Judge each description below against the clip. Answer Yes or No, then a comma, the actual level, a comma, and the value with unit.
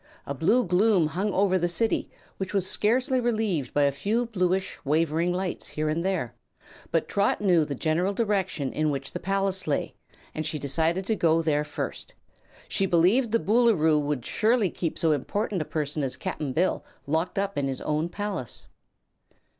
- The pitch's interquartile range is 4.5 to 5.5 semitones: Yes, average, 4.8 semitones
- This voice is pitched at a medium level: Yes, medium, 175 Hz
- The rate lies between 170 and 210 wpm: Yes, average, 180 wpm